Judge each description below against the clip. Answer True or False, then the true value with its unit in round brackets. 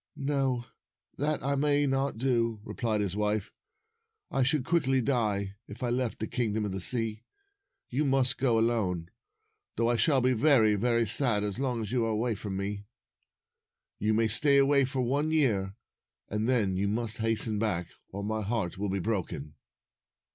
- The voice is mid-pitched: False (115 Hz)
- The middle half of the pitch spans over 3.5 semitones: True (4.3 semitones)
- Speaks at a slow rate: False (175 wpm)